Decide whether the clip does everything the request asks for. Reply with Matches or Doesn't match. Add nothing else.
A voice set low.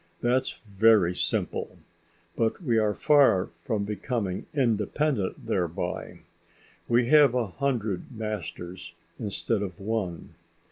Matches